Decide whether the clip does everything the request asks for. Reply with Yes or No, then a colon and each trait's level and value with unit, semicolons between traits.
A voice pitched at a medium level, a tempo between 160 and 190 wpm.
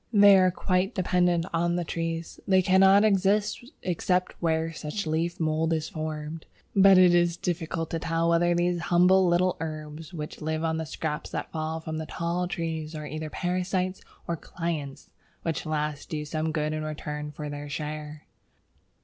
Yes: medium, 165 Hz; average, 175 wpm